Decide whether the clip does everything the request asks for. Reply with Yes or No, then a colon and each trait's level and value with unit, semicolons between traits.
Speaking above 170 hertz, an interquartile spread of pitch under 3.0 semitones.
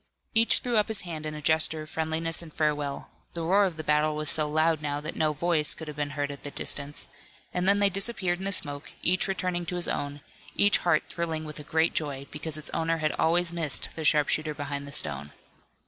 No: medium, 155 Hz; narrow, 2.6 semitones